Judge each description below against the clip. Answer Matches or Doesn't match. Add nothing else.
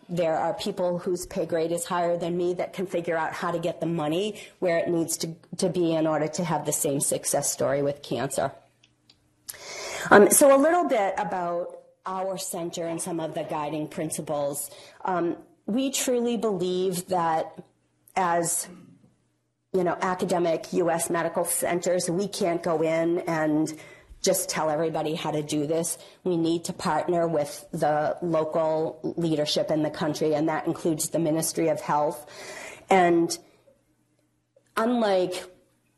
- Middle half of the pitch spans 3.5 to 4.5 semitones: Doesn't match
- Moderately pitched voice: Matches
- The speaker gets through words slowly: Doesn't match